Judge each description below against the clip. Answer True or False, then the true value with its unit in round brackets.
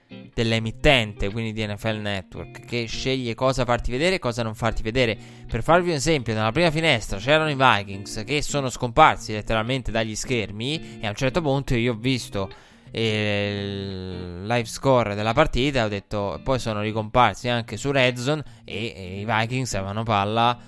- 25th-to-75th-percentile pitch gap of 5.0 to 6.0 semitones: False (3.5 semitones)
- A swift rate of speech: True (175 wpm)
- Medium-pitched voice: False (115 Hz)